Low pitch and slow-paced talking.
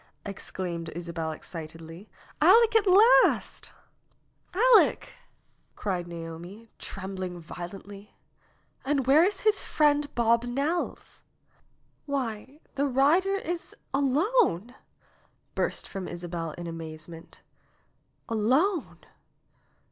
No: high, 225 Hz; slow, 95 wpm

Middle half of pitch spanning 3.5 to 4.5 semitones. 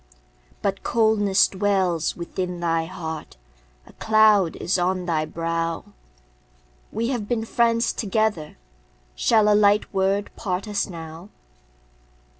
Yes: average, 3.9 semitones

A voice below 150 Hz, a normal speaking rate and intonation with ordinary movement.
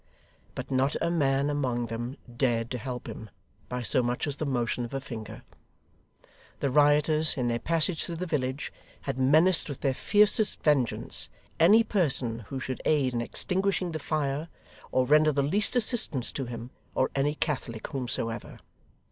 Yes: low, 135 Hz; average, 165 wpm; average, 4.0 semitones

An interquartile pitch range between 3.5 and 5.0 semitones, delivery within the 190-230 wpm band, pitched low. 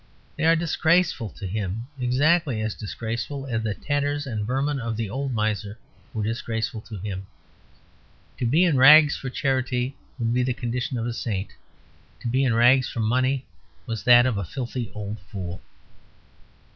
No: average, 3.8 semitones; average, 170 wpm; low, 120 Hz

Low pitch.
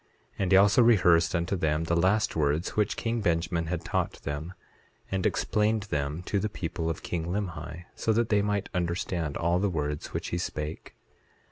Yes: very low, 85 Hz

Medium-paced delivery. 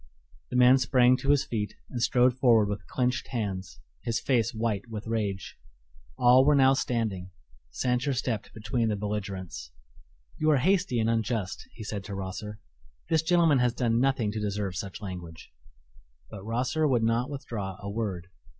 Yes: average, 165 wpm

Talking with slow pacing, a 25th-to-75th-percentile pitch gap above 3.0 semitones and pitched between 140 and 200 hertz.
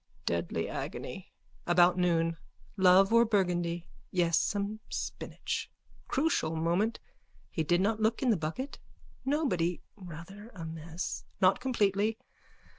Yes: slow, 115 wpm; average, 4.4 semitones; medium, 185 Hz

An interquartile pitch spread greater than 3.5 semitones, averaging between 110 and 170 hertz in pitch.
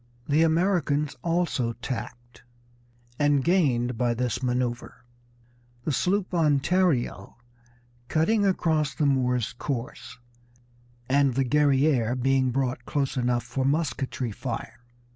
Yes: average, 4.0 semitones; low, 135 Hz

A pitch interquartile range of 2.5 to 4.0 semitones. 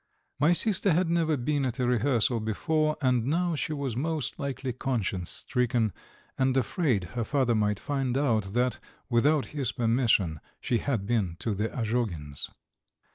No: average, 4.5 semitones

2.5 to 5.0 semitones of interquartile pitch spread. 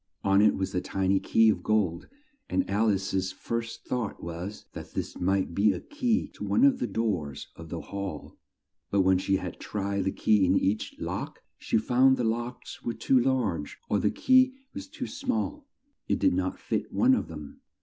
No: wide, 5.4 semitones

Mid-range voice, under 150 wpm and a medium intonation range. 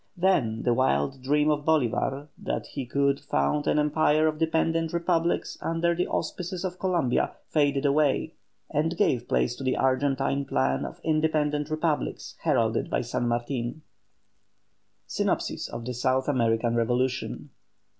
Yes: medium, 145 Hz; average, 140 wpm; average, 4.0 semitones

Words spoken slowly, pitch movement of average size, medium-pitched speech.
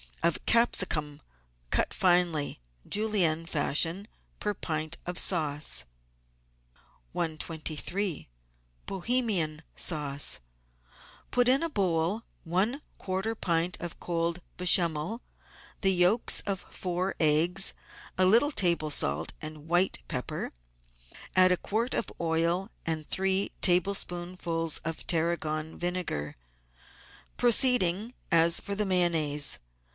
Yes: slow, 100 wpm; average, 3.3 semitones; medium, 175 Hz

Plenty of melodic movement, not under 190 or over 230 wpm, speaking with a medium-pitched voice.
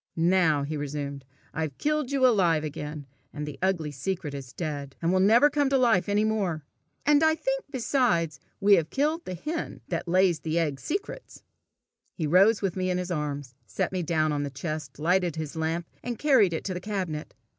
Yes: wide, 6.1 semitones; average, 200 wpm; medium, 175 Hz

